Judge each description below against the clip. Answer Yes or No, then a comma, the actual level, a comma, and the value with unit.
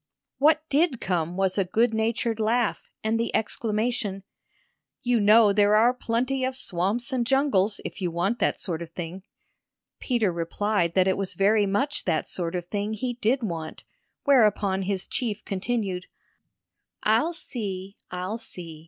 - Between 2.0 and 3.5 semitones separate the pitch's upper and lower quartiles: No, average, 4.2 semitones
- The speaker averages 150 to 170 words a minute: Yes, average, 155 wpm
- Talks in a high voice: Yes, high, 210 Hz